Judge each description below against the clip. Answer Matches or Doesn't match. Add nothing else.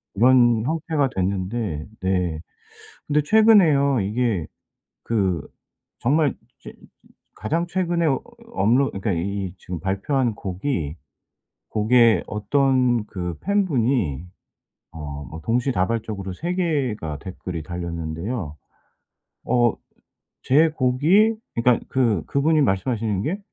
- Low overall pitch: Matches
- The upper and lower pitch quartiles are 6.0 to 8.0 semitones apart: Matches